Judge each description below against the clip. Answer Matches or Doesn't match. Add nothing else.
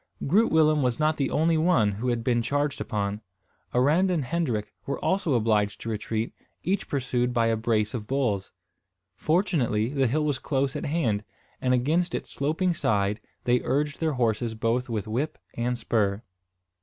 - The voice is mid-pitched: Doesn't match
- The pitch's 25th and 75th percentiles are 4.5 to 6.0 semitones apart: Matches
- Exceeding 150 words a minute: Matches